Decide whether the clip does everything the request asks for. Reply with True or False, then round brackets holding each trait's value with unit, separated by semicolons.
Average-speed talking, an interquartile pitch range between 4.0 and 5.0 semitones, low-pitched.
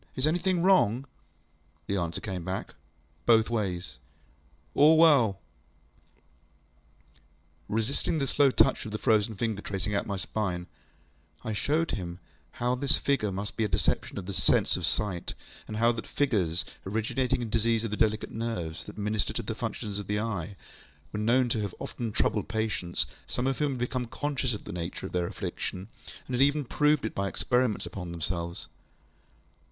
True (175 wpm; 4.6 semitones; 110 Hz)